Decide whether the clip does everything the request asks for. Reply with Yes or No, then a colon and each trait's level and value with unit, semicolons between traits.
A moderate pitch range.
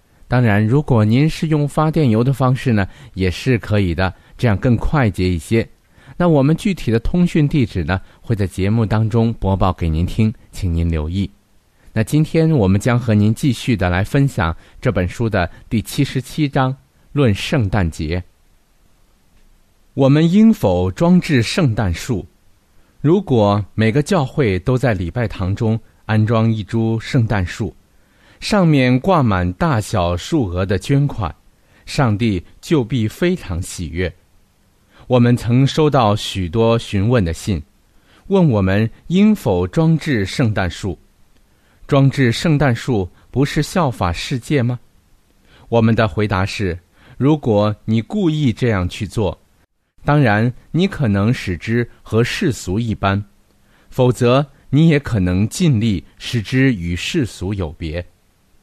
No: wide, 5.8 semitones